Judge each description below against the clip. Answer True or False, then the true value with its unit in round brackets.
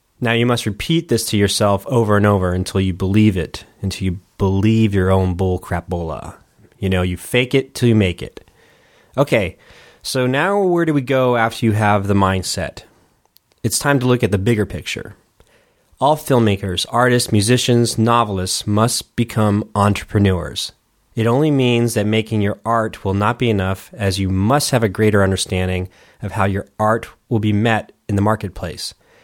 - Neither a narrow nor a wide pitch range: True (3.5 semitones)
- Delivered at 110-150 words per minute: False (180 wpm)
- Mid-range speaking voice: False (105 Hz)